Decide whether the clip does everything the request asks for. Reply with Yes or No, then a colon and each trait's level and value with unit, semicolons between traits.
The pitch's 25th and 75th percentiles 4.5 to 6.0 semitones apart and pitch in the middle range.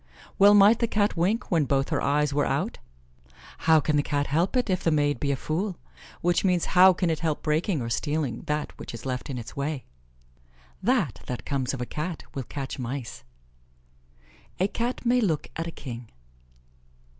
Yes: average, 5.0 semitones; medium, 155 Hz